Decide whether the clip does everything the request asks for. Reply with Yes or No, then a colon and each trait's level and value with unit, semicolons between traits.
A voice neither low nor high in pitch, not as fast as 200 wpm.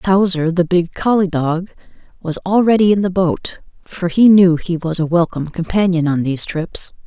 Yes: medium, 175 Hz; average, 180 wpm